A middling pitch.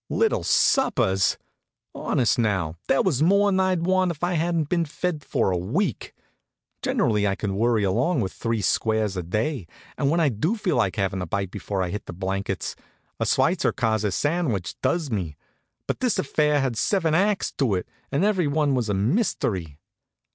No: low, 120 Hz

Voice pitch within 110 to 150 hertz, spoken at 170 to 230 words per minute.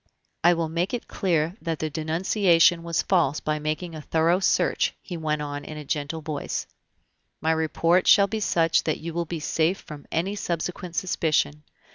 No: medium, 165 Hz; average, 180 wpm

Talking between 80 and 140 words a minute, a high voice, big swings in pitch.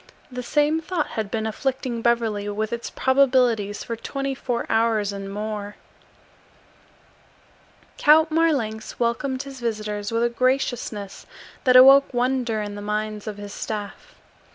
No: slow, 135 wpm; high, 235 Hz; average, 3.8 semitones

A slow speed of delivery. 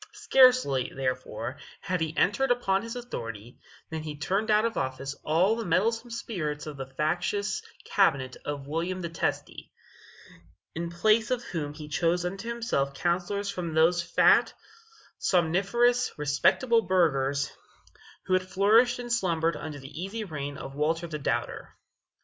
No: average, 145 wpm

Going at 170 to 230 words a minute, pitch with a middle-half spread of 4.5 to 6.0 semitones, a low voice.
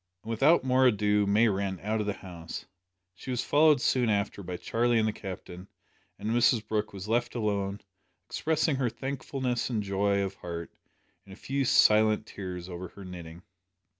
No: average, 175 wpm; average, 3.8 semitones; low, 105 Hz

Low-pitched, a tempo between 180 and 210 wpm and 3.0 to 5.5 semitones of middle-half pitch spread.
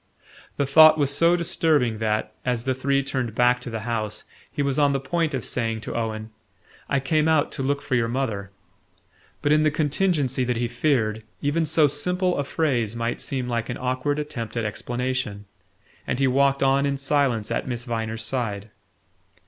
Yes: low, 130 Hz; average, 185 wpm; average, 3.8 semitones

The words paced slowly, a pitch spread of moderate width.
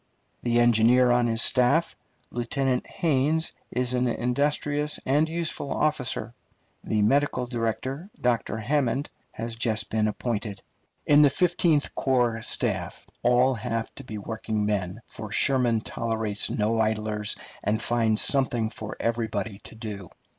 Yes: slow, 130 wpm; average, 3.3 semitones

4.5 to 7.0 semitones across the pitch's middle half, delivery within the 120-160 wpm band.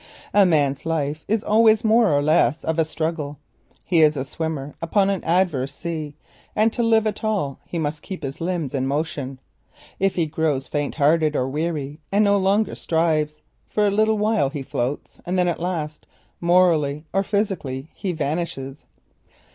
No: average, 4.8 semitones; average, 170 wpm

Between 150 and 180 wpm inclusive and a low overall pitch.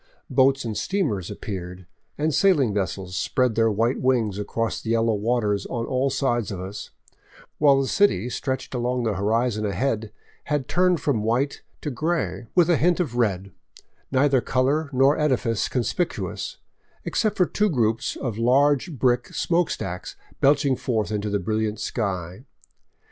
Yes: average, 155 wpm; low, 120 Hz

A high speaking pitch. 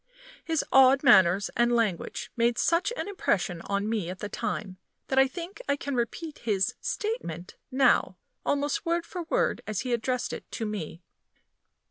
Yes: high, 240 Hz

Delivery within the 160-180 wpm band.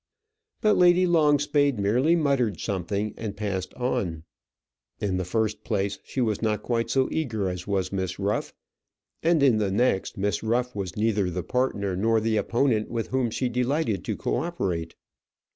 Yes: average, 165 wpm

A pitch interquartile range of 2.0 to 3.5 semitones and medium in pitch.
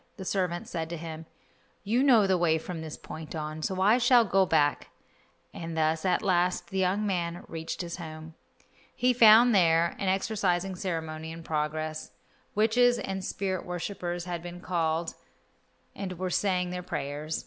Yes: average, 3.1 semitones; medium, 175 Hz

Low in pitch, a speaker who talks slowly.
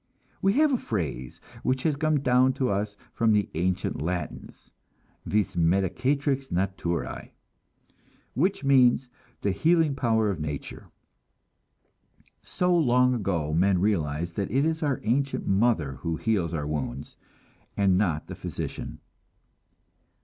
Yes: low, 105 Hz; slow, 125 wpm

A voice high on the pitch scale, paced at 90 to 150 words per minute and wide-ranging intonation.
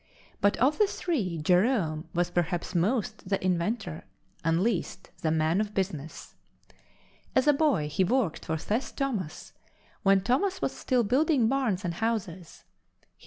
Yes: high, 195 Hz; average, 145 wpm; wide, 6.5 semitones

